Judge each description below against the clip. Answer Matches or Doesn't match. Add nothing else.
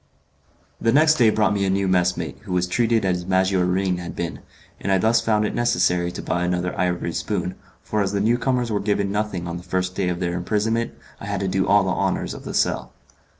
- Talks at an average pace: Doesn't match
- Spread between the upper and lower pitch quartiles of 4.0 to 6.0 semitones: Doesn't match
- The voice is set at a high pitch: Doesn't match